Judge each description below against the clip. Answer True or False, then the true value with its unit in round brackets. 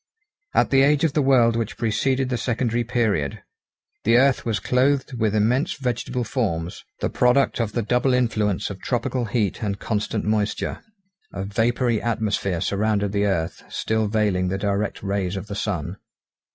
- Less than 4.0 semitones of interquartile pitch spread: True (3.5 semitones)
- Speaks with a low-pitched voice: True (110 Hz)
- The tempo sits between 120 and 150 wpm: False (165 wpm)